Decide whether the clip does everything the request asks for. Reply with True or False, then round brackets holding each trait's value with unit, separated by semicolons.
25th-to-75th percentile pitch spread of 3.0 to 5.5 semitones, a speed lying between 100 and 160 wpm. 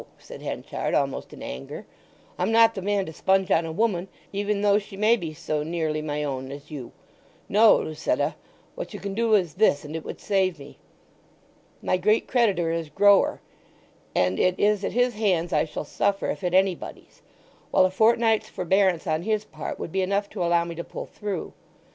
False (4.3 semitones; 195 wpm)